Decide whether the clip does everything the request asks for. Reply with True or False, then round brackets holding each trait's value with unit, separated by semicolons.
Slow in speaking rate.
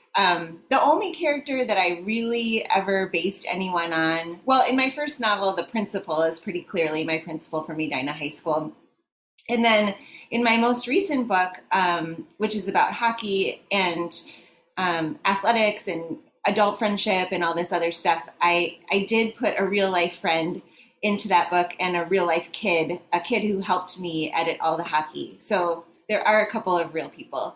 False (180 wpm)